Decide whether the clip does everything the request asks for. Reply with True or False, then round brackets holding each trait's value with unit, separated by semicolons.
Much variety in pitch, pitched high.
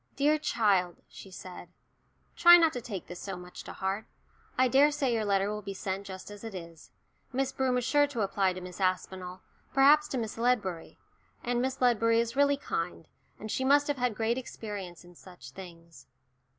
True (5.8 semitones; 215 Hz)